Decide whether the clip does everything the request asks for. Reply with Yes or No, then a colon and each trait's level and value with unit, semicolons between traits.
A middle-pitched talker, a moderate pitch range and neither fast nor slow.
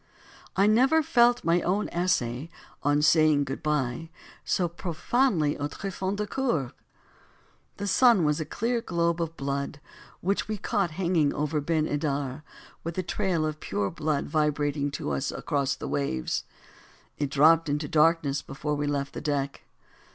Yes: medium, 155 Hz; average, 4.1 semitones; average, 155 wpm